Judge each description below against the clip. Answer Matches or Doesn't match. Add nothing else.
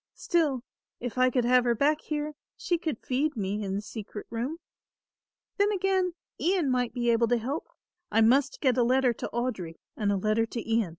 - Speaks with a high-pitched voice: Matches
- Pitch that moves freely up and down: Doesn't match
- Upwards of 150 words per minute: Matches